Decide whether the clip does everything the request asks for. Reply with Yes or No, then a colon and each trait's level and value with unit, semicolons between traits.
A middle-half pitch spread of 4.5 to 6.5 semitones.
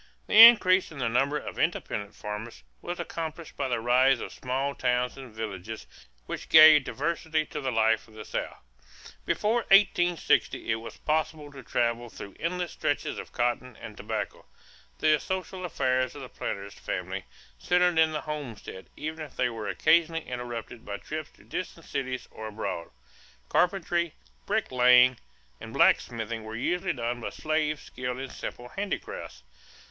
Yes: wide, 5.4 semitones